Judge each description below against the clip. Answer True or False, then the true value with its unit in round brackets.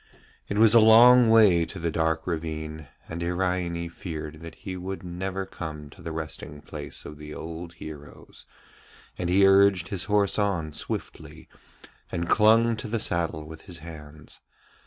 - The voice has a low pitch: True (85 Hz)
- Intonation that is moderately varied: True (3.7 semitones)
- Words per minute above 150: True (160 wpm)